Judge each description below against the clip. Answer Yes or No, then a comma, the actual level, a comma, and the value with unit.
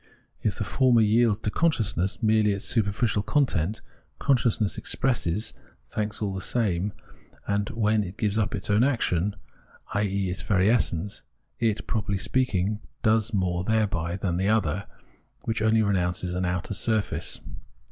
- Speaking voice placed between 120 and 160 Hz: No, low, 105 Hz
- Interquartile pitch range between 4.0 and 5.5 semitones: No, average, 2.7 semitones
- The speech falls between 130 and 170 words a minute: Yes, average, 145 wpm